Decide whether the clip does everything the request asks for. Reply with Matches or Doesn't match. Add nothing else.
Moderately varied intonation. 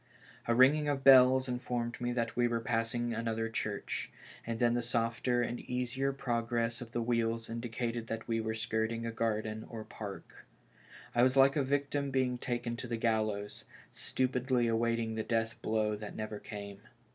Doesn't match